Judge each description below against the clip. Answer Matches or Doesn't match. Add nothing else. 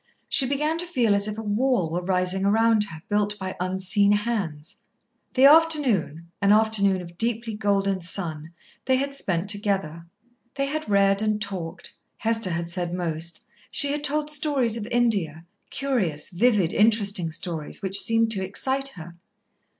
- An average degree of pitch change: Matches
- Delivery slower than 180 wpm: Matches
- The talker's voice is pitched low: Doesn't match